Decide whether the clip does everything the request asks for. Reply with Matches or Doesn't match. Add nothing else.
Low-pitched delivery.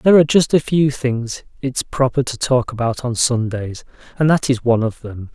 Matches